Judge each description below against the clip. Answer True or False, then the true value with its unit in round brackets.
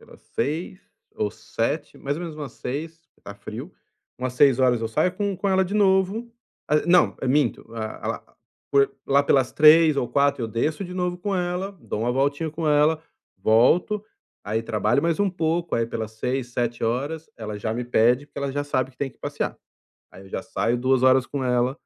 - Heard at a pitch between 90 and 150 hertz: True (140 Hz)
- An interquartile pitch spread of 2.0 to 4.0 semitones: False (5.5 semitones)